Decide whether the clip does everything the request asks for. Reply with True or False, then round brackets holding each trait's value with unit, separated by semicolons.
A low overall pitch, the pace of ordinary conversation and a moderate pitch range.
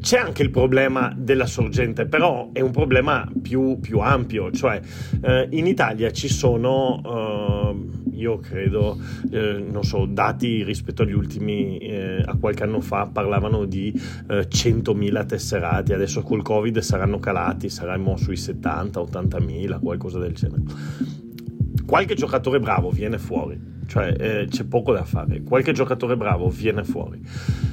True (120 Hz; 145 wpm; 3.5 semitones)